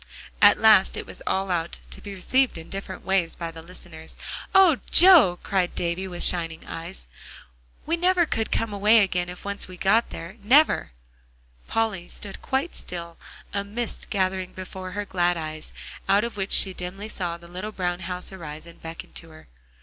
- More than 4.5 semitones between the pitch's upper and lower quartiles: No, average, 3.2 semitones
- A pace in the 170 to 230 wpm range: Yes, average, 180 wpm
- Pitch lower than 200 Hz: Yes, medium, 185 Hz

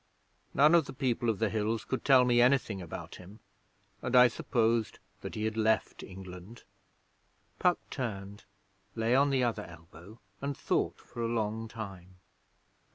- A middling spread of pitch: Yes, average, 3.5 semitones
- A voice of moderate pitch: No, low, 115 Hz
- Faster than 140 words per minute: Yes, average, 160 wpm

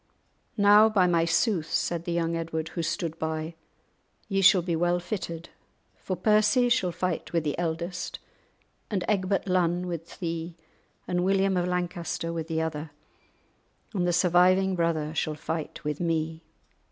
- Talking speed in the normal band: Yes, average, 155 wpm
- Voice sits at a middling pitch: Yes, medium, 175 Hz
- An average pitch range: No, narrow, 2.1 semitones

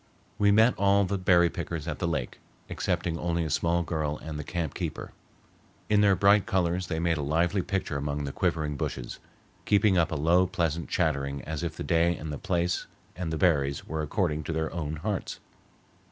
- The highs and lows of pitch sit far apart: No, average, 3.0 semitones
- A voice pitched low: Yes, very low, 85 Hz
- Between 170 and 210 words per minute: Yes, average, 195 wpm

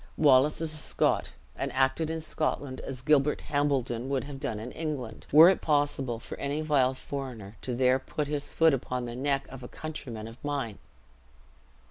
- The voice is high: No, low, 135 Hz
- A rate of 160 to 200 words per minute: Yes, average, 180 wpm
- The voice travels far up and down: No, average, 2.8 semitones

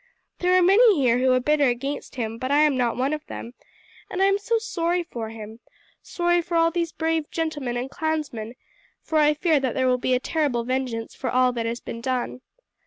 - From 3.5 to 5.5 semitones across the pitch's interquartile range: Yes, average, 5.1 semitones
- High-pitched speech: Yes, very high, 275 Hz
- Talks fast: Yes, fast, 215 wpm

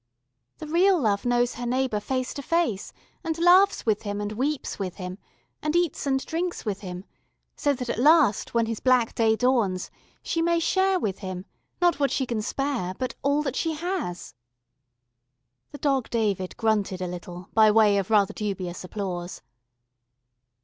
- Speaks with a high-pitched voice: Yes, high, 235 Hz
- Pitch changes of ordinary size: No, wide, 6.6 semitones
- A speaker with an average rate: Yes, average, 170 wpm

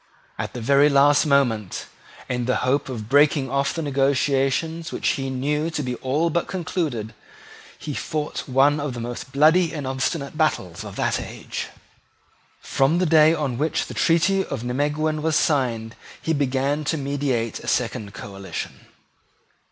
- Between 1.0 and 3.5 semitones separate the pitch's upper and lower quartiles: Yes, average, 3.2 semitones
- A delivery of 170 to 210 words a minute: No, average, 160 wpm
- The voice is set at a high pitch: No, medium, 140 Hz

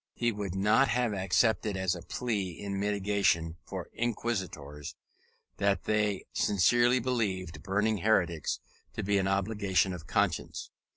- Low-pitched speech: Yes, low, 100 Hz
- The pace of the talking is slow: Yes, slow, 130 wpm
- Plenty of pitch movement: No, average, 2.7 semitones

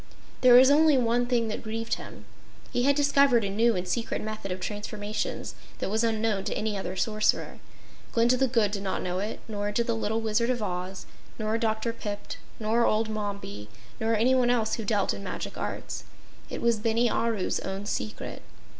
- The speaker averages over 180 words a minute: Yes, average, 190 wpm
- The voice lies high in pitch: Yes, high, 220 Hz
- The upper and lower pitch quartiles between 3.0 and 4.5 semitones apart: No, narrow, 2.4 semitones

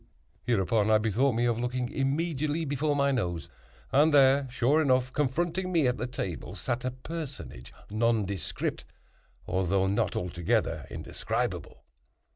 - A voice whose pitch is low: Yes, low, 125 Hz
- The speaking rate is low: Yes, slow, 130 wpm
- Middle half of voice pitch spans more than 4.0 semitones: Yes, average, 4.9 semitones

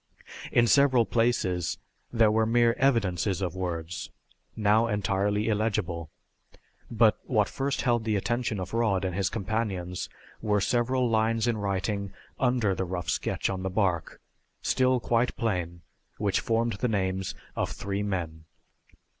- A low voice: Yes, low, 105 Hz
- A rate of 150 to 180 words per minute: No, average, 140 wpm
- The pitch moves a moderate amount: Yes, average, 3.7 semitones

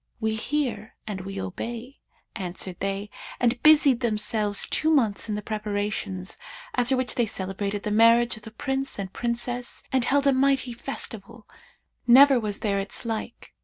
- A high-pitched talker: Yes, high, 225 Hz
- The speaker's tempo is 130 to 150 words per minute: No, average, 160 wpm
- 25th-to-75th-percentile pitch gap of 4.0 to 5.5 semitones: No, average, 3.5 semitones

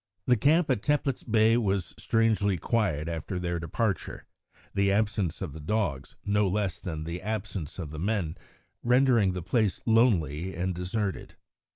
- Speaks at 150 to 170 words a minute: Yes, average, 155 wpm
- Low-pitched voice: Yes, low, 100 Hz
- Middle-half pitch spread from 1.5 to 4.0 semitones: No, average, 4.5 semitones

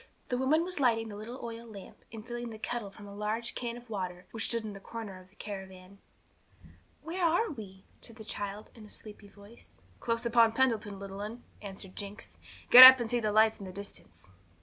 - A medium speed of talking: No, fast, 215 wpm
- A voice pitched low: No, high, 220 Hz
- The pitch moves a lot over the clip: No, average, 3.0 semitones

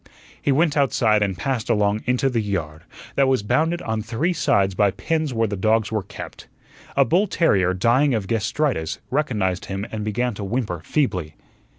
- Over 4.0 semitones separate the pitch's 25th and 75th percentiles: Yes, wide, 5.4 semitones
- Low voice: Yes, low, 110 Hz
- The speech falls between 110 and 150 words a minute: No, average, 180 wpm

